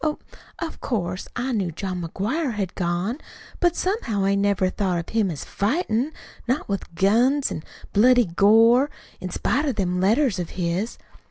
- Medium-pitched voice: No, high, 205 Hz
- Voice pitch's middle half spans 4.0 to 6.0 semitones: Yes, wide, 5.5 semitones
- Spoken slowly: No, average, 165 wpm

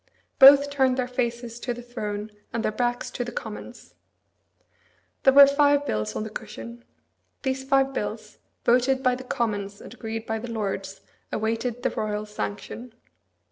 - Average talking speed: Yes, average, 165 wpm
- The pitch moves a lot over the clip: No, average, 3.2 semitones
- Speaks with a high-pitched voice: Yes, high, 240 Hz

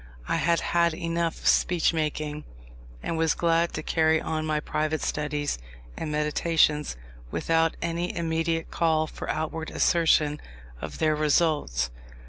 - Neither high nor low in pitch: Yes, medium, 160 Hz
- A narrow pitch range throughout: Yes, narrow, 1.6 semitones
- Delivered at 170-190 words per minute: No, slow, 135 wpm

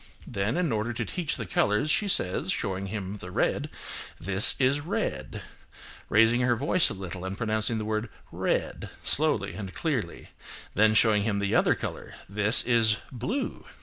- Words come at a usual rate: Yes, average, 165 wpm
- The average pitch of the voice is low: Yes, low, 110 Hz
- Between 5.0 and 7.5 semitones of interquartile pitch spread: No, average, 3.9 semitones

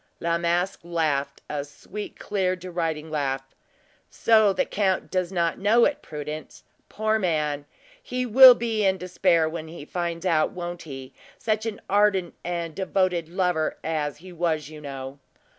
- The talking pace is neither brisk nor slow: Yes, average, 160 wpm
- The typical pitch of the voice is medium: Yes, medium, 175 Hz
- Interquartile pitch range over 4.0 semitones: No, average, 3.7 semitones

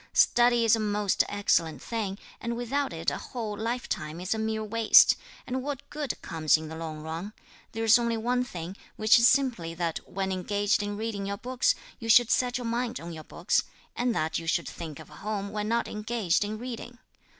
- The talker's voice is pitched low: No, high, 215 Hz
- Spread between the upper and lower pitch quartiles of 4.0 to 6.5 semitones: Yes, average, 5.1 semitones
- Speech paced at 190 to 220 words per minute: Yes, average, 200 wpm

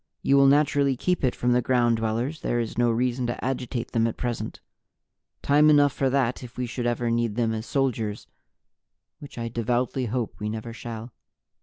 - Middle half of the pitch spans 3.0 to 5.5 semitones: No, narrow, 2.4 semitones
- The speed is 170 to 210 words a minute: Yes, average, 190 wpm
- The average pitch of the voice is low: Yes, low, 120 Hz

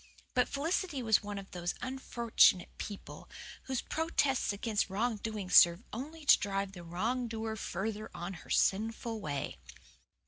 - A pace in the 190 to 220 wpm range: No, average, 145 wpm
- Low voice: No, high, 220 Hz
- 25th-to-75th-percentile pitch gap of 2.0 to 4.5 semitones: Yes, average, 4.1 semitones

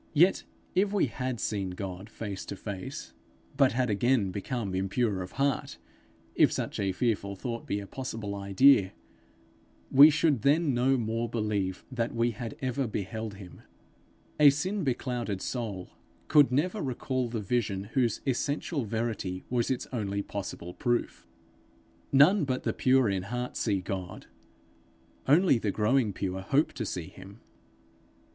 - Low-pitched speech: Yes, low, 115 Hz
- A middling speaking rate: Yes, average, 150 wpm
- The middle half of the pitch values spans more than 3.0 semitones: Yes, average, 5.0 semitones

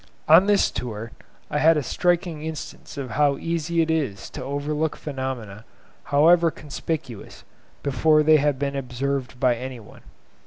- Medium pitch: Yes, medium, 145 Hz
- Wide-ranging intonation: No, average, 3.6 semitones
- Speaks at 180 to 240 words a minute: No, average, 150 wpm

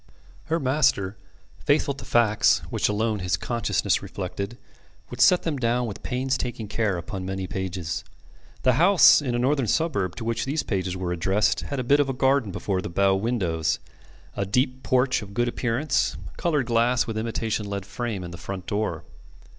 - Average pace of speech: Yes, average, 175 wpm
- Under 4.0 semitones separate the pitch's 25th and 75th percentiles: No, average, 5.1 semitones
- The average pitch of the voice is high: No, low, 115 Hz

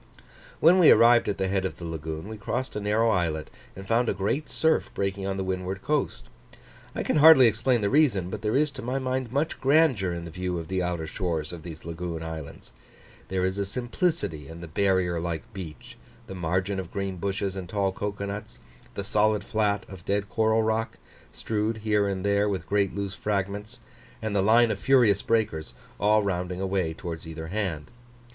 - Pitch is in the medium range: No, low, 100 Hz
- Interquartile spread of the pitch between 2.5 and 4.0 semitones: Yes, average, 3.7 semitones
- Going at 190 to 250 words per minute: Yes, average, 200 wpm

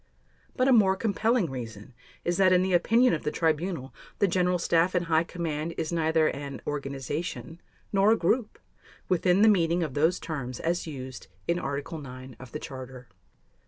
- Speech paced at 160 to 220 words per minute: Yes, average, 175 wpm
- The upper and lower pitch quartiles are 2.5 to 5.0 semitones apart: Yes, average, 4.6 semitones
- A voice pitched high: No, medium, 165 Hz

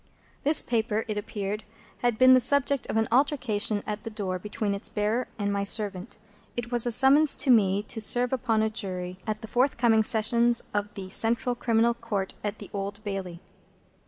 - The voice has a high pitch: Yes, high, 220 Hz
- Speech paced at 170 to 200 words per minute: Yes, average, 190 wpm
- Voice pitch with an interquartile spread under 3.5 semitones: Yes, average, 2.8 semitones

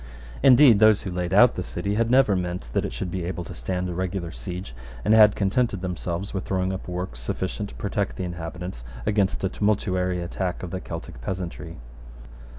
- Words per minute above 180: Yes, average, 195 wpm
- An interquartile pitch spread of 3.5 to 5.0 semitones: No, narrow, 2.4 semitones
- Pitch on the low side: Yes, very low, 95 Hz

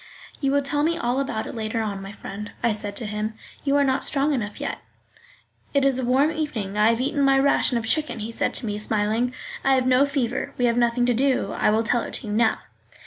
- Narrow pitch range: No, average, 4.1 semitones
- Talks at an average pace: No, fast, 250 wpm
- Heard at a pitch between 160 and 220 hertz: No, high, 245 Hz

